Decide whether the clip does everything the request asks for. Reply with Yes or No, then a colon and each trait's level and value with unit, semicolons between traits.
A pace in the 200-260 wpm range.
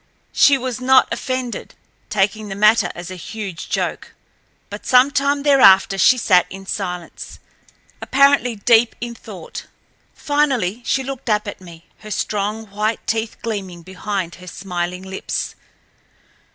No: average, 140 wpm